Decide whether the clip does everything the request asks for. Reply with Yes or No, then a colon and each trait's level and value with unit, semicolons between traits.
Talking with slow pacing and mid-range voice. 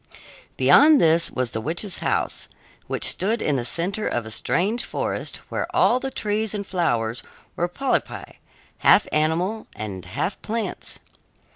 No: average, 145 wpm; medium, 175 Hz